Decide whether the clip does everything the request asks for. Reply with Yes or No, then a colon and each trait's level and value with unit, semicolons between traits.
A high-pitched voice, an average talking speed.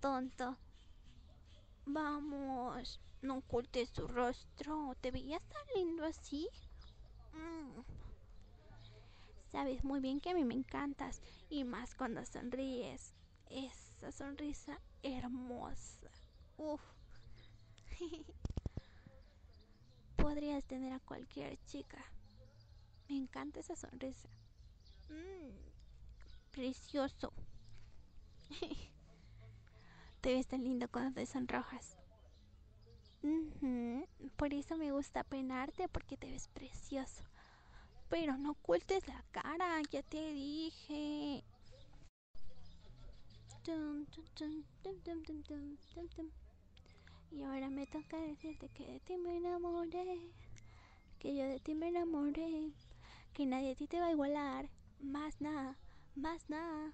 No: very high, 270 Hz; slow, 95 wpm